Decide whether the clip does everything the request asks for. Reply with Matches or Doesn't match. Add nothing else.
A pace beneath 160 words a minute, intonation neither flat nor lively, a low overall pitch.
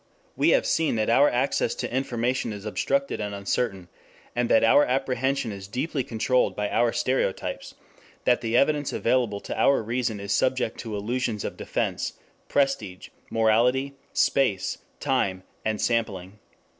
Matches